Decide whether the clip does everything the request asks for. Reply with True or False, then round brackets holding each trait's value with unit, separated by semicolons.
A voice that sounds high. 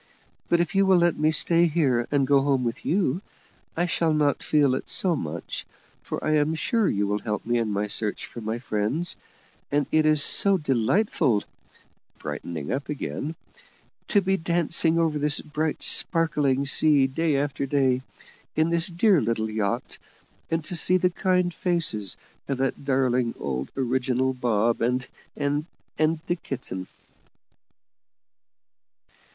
False (145 Hz)